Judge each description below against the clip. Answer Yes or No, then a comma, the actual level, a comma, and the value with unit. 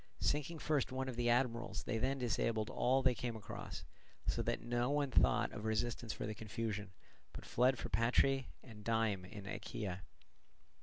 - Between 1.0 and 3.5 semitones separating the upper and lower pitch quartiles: Yes, average, 3.2 semitones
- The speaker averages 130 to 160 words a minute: No, average, 170 wpm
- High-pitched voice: No, low, 120 Hz